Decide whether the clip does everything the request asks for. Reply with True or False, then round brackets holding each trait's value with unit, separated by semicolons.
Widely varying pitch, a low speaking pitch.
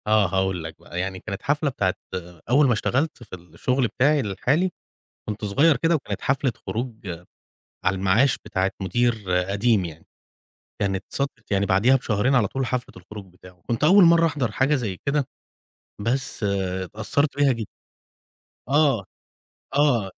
True (6.1 semitones; 115 Hz)